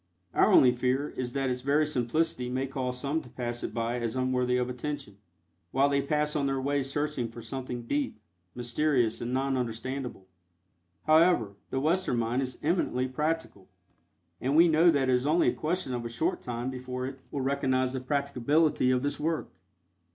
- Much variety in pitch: No, average, 2.8 semitones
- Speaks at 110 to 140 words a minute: No, average, 185 wpm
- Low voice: Yes, low, 130 Hz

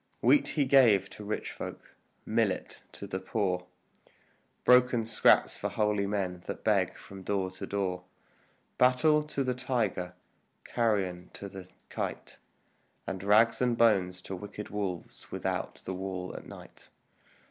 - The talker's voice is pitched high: No, low, 100 Hz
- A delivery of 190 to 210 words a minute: No, average, 140 wpm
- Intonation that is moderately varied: Yes, average, 4.0 semitones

